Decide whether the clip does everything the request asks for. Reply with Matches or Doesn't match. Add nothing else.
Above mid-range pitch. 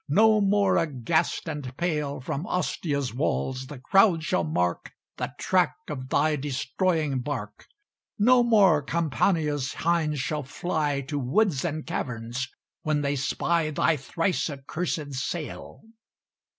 Doesn't match